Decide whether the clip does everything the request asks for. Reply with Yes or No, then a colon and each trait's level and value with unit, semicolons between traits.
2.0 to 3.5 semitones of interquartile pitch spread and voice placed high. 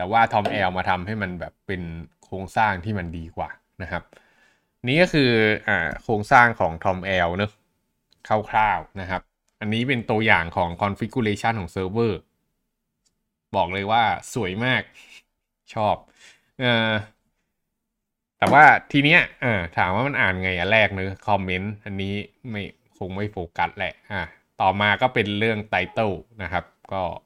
No: average, 3.1 semitones; low, 105 Hz